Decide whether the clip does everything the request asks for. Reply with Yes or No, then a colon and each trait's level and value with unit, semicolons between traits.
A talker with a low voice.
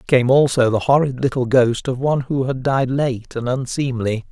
Yes: low, 130 Hz